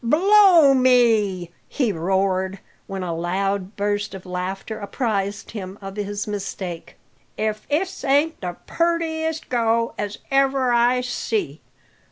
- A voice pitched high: Yes, high, 210 Hz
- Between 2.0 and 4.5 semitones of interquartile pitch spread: No, average, 5.2 semitones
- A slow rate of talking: Yes, slow, 125 wpm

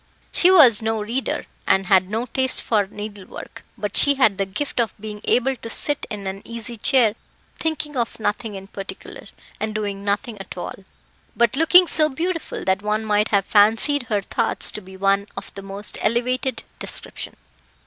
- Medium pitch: No, high, 215 Hz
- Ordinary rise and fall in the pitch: Yes, average, 4.0 semitones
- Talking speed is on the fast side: No, average, 175 wpm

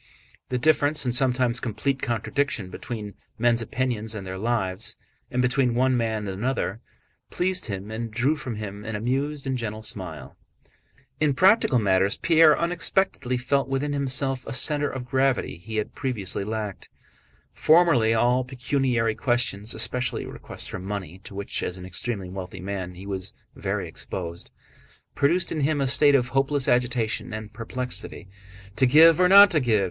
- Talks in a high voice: No, low, 120 Hz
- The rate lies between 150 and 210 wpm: Yes, average, 160 wpm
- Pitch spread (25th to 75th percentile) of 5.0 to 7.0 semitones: No, average, 4.6 semitones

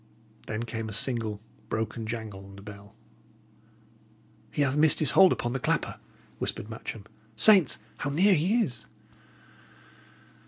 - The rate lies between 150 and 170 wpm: No, average, 140 wpm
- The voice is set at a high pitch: No, low, 115 Hz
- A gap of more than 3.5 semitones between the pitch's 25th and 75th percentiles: Yes, wide, 5.5 semitones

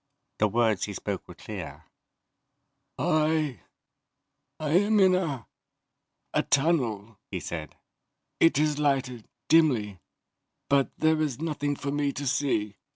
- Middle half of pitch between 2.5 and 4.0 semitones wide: No, wide, 5.4 semitones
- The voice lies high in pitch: No, medium, 140 Hz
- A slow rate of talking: Yes, slow, 120 wpm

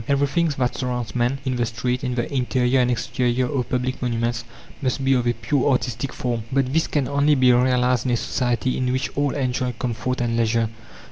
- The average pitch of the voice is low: Yes, low, 125 Hz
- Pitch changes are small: Yes, narrow, 1.6 semitones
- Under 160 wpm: No, fast, 205 wpm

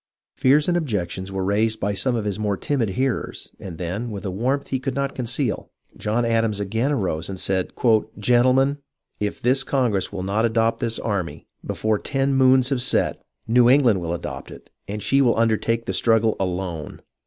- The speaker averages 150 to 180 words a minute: No, average, 190 wpm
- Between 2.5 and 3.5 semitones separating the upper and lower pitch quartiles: No, average, 4.5 semitones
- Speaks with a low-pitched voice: Yes, low, 115 Hz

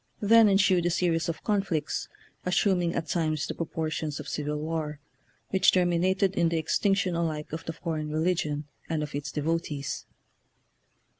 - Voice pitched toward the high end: No, medium, 165 Hz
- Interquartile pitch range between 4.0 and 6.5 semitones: No, average, 2.9 semitones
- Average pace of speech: Yes, average, 150 wpm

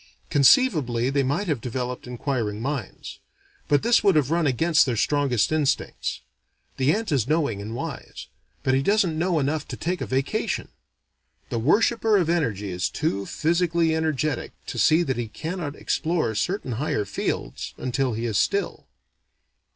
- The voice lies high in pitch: No, medium, 145 Hz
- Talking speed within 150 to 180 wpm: Yes, average, 160 wpm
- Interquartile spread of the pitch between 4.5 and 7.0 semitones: Yes, average, 5.3 semitones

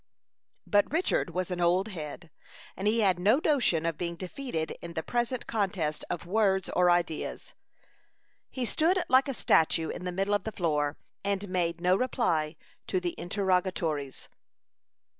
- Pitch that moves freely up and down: No, average, 3.9 semitones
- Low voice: No, medium, 185 Hz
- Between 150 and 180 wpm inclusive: Yes, average, 160 wpm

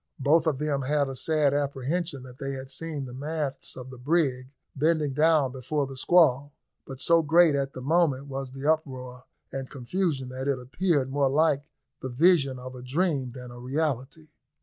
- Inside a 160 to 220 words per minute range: Yes, average, 185 wpm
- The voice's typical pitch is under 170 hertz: Yes, medium, 140 Hz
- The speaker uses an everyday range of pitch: Yes, average, 3.2 semitones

